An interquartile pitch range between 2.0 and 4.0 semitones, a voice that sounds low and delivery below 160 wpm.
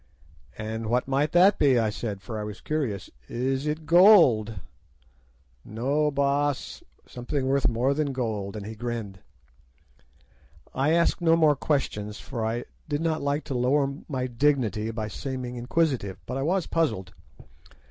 No: average, 4.8 semitones; low, 130 Hz; average, 150 wpm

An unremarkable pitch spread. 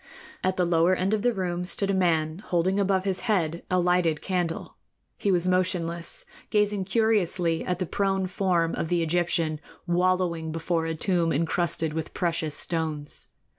No: narrow, 2.2 semitones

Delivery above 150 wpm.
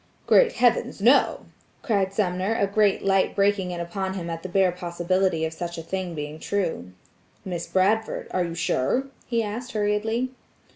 Yes: average, 165 wpm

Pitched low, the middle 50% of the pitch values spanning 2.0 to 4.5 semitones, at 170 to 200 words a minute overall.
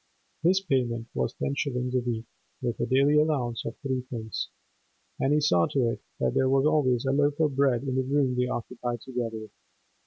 Yes: low, 130 Hz; average, 2.9 semitones; average, 195 wpm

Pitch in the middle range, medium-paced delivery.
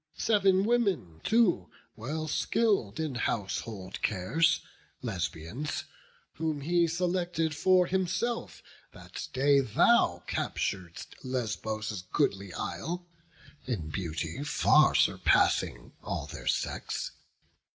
No: medium, 145 Hz; slow, 95 wpm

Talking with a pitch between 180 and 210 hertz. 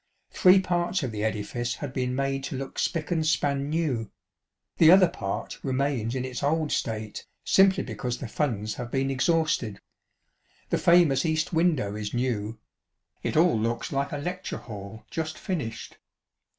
No: low, 135 Hz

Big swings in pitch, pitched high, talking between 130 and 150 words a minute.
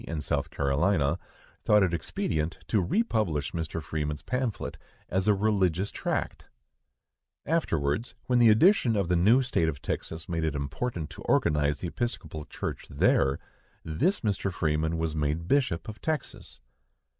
No: wide, 6.1 semitones; very low, 85 Hz; average, 145 wpm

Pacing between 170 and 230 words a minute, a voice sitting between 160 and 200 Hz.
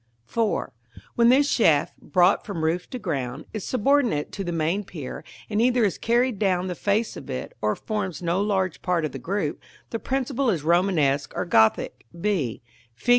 Yes: average, 185 wpm; medium, 185 Hz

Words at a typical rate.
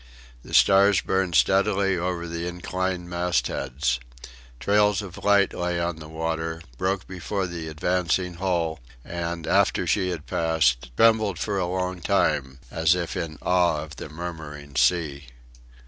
Yes: average, 145 wpm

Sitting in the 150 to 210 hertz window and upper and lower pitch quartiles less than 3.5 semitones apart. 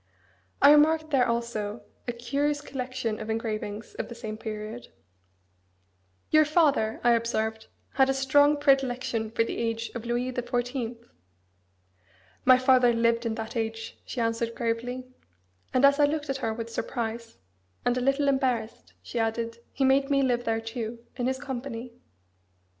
No: high, 240 Hz; average, 2.8 semitones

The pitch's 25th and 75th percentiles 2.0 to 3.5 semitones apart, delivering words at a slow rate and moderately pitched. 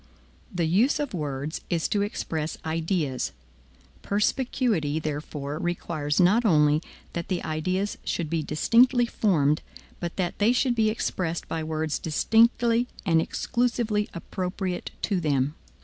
No: wide, 5.5 semitones; slow, 130 wpm; medium, 175 Hz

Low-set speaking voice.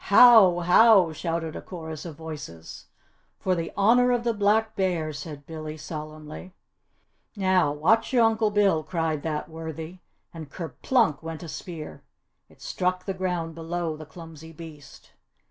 No: medium, 165 Hz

